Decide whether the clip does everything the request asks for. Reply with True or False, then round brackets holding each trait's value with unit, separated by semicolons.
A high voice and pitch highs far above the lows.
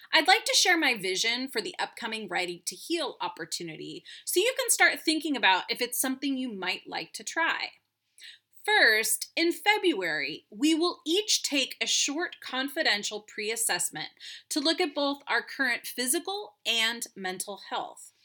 True (290 Hz; 7.6 semitones)